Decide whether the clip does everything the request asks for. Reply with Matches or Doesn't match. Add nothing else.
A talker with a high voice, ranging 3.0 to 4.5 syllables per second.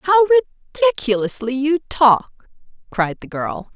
Matches